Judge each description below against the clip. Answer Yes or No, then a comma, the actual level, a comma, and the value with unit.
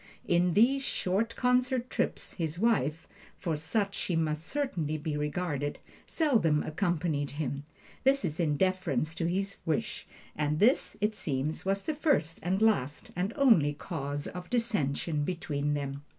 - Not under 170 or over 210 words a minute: No, average, 145 wpm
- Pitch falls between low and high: Yes, medium, 170 Hz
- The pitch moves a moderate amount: No, wide, 5.9 semitones